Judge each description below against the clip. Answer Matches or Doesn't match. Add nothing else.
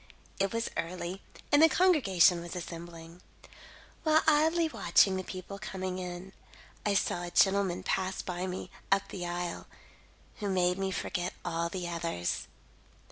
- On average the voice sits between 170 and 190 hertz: Matches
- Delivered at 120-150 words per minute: Matches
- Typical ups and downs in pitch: Doesn't match